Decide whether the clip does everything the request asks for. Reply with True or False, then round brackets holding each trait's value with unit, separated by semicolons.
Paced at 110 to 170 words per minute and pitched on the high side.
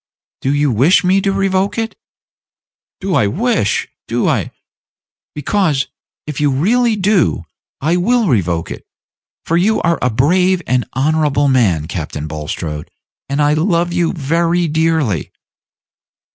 False (140 wpm; 155 Hz)